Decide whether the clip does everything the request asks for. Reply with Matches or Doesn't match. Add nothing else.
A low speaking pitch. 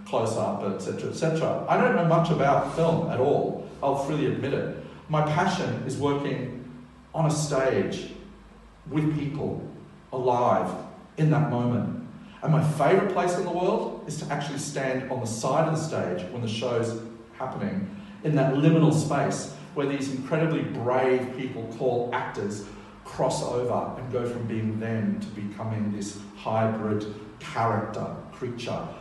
Matches